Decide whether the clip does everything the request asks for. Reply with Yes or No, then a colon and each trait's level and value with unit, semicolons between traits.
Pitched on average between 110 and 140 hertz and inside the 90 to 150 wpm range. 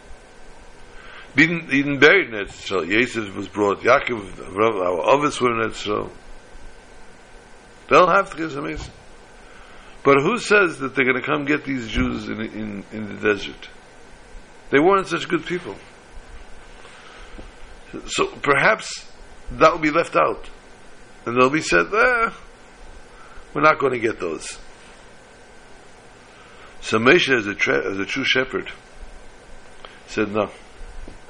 Yes: low, 135 Hz; slow, 135 wpm